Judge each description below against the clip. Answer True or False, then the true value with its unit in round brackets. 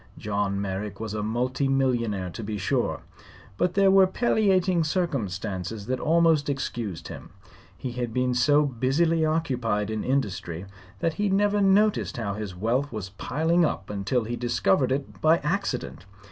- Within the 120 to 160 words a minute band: True (155 wpm)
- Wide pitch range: True (7.5 semitones)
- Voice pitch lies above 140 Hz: False (125 Hz)